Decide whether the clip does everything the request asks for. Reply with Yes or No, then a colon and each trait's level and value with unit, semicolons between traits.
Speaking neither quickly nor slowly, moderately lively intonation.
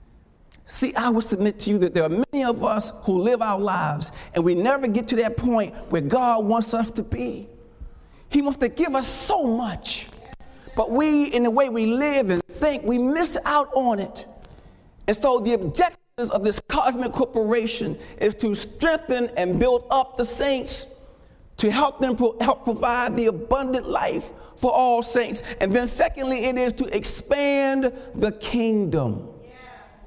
Yes: average, 175 wpm; average, 3.6 semitones